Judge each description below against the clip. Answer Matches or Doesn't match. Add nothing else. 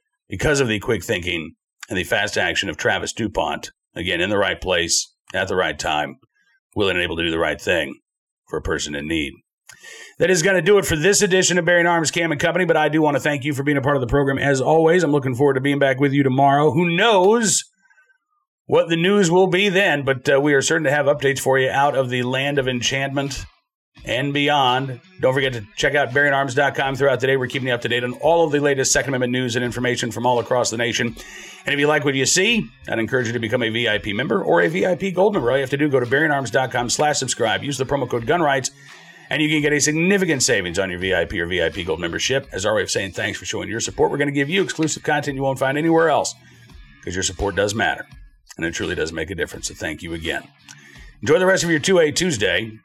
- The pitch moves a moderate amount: Matches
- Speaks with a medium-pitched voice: Matches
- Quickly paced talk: Matches